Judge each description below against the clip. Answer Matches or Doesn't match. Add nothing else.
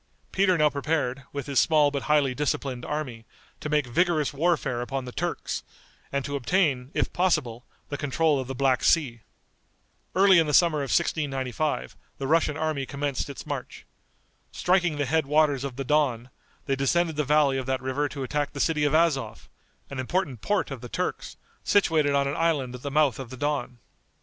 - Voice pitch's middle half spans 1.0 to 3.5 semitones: Matches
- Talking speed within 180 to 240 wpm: Matches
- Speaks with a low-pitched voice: Doesn't match